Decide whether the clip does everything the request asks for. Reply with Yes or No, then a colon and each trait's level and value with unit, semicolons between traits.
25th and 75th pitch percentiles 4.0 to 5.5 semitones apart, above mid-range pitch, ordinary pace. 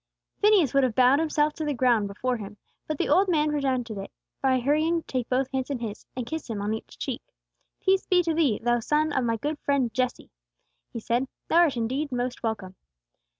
No: average, 4.4 semitones; very high, 260 Hz; fast, 215 wpm